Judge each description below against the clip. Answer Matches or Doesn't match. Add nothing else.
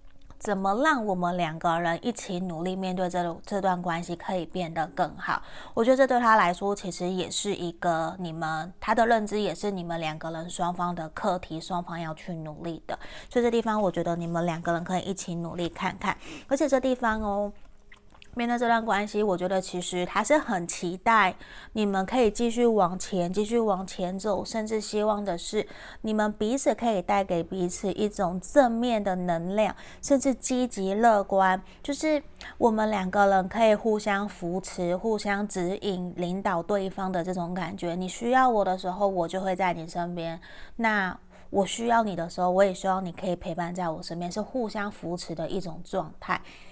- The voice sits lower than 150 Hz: Doesn't match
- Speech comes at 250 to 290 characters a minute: Matches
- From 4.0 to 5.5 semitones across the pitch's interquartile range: Doesn't match